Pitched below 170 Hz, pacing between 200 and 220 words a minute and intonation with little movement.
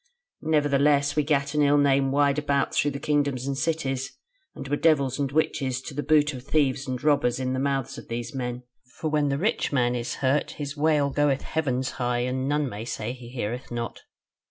Yes: medium, 140 Hz; fast, 205 wpm; narrow, 2.2 semitones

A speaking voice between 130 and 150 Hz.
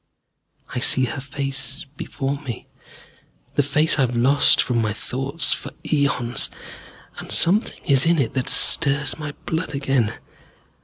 Yes: low, 135 Hz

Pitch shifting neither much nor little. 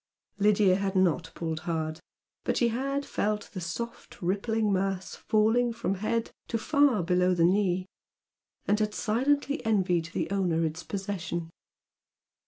Yes: average, 3.9 semitones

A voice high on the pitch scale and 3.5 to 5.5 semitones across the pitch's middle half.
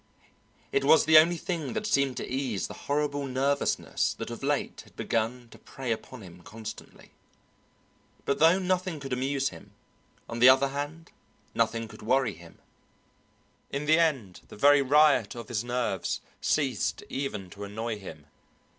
No: low, 135 Hz; average, 4.5 semitones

